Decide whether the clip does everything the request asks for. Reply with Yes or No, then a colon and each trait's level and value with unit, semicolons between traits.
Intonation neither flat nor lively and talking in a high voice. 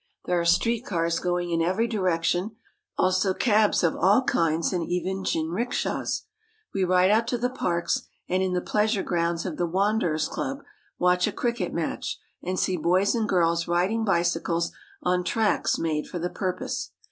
No: average, 3.5 semitones; medium, 180 Hz